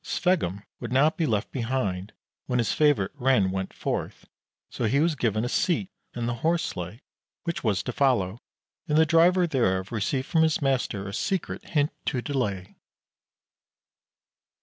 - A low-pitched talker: Yes, low, 125 Hz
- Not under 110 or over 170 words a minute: Yes, average, 160 wpm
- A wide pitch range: Yes, wide, 7.1 semitones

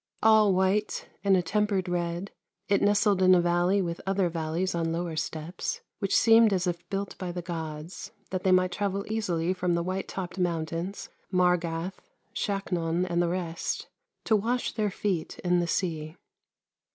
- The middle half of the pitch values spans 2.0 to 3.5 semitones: Yes, narrow, 2.5 semitones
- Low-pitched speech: No, medium, 180 Hz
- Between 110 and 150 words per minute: No, average, 170 wpm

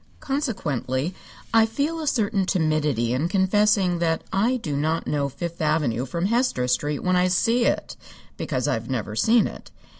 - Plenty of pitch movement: Yes, wide, 6.9 semitones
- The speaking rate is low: No, average, 160 wpm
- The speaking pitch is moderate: Yes, medium, 180 Hz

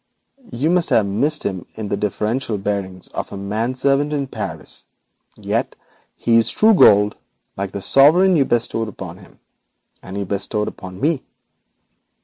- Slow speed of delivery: No, average, 155 wpm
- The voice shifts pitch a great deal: Yes, wide, 5.8 semitones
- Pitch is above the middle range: No, low, 110 Hz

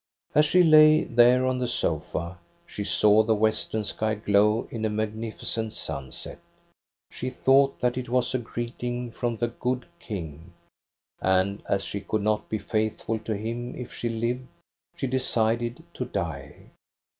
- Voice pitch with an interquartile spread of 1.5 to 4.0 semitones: Yes, average, 2.8 semitones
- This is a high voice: No, low, 115 Hz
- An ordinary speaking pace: Yes, average, 155 wpm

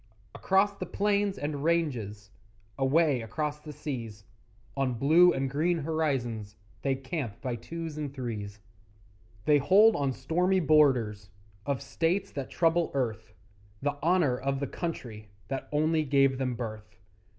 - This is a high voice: No, medium, 140 Hz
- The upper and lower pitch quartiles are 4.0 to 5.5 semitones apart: Yes, average, 4.9 semitones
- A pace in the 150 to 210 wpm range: No, average, 140 wpm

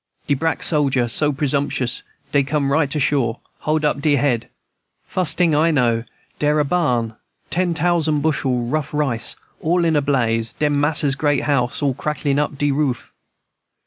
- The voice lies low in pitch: No, medium, 145 Hz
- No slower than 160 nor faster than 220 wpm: Yes, average, 170 wpm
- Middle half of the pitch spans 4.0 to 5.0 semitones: No, average, 2.7 semitones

